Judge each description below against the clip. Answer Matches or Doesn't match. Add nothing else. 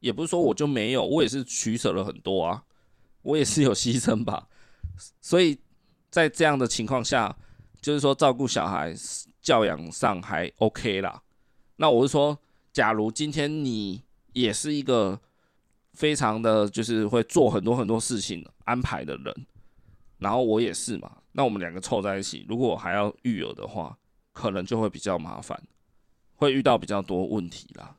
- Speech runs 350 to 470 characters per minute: Doesn't match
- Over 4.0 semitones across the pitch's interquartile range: Matches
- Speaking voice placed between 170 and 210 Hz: Doesn't match